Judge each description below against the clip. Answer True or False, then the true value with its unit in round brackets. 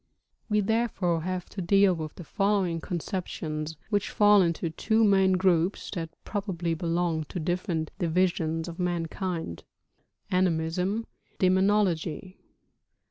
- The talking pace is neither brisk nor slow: False (125 wpm)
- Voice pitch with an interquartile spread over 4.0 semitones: False (3.0 semitones)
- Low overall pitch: False (180 Hz)